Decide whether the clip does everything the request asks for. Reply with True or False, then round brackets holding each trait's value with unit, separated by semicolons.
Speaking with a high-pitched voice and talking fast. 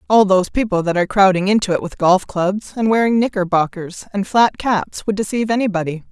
False (195 Hz; 195 wpm)